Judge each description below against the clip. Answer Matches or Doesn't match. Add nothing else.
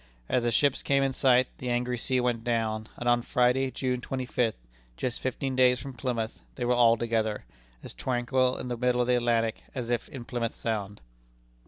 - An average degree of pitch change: Doesn't match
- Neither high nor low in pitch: Doesn't match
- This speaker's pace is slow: Doesn't match